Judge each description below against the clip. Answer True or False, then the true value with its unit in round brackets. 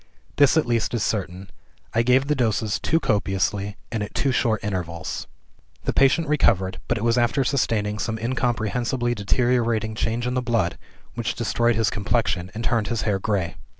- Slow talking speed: False (175 wpm)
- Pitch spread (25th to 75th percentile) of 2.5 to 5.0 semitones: True (2.9 semitones)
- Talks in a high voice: False (115 Hz)